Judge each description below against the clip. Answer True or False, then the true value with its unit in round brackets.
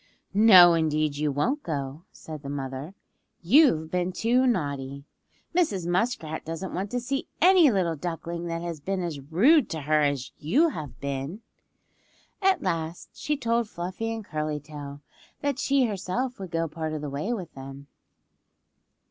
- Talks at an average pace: True (160 wpm)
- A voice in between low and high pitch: True (170 Hz)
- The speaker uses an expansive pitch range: True (7.2 semitones)